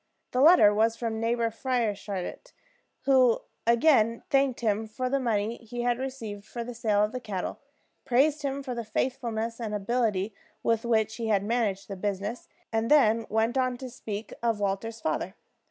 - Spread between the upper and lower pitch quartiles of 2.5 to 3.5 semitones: Yes, average, 2.9 semitones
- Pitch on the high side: Yes, high, 230 Hz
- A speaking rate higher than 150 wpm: Yes, average, 170 wpm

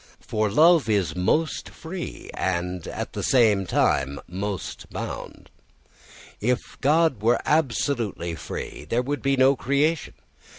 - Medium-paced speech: No, slow, 125 wpm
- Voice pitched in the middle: No, low, 120 Hz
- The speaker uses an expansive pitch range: Yes, wide, 7.0 semitones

